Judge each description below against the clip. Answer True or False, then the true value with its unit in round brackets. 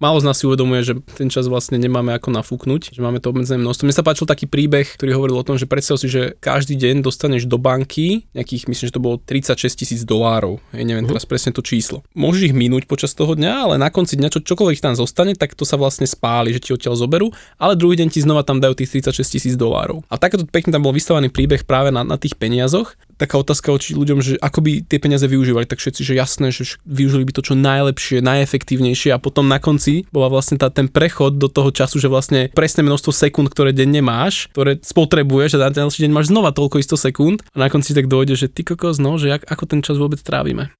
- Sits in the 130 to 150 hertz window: True (140 Hz)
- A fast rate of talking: True (240 wpm)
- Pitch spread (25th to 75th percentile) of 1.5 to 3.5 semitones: True (2.5 semitones)